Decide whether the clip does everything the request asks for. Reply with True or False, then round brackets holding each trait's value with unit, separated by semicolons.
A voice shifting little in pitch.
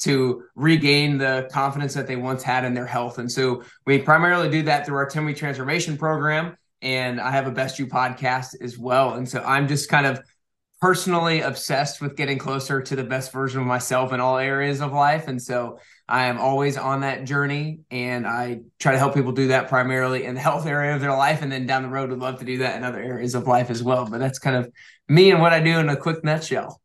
True (2.3 semitones)